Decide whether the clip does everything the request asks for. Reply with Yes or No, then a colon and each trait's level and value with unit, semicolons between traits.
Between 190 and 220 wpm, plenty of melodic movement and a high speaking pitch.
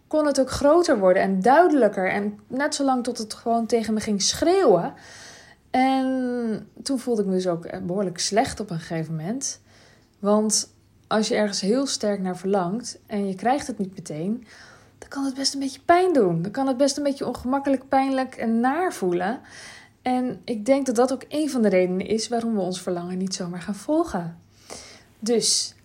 Yes: average, 195 wpm; wide, 5.7 semitones; high, 230 Hz